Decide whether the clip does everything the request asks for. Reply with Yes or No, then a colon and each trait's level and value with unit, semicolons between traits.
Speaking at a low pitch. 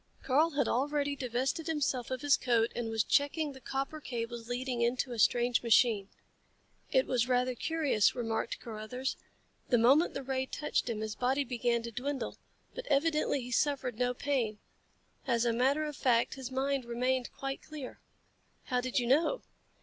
No: very high, 255 Hz